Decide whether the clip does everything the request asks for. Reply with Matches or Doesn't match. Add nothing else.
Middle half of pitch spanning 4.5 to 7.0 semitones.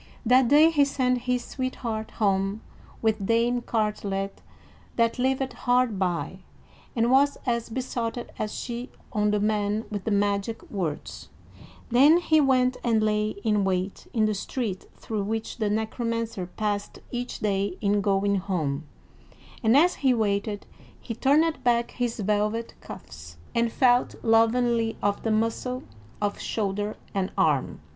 Doesn't match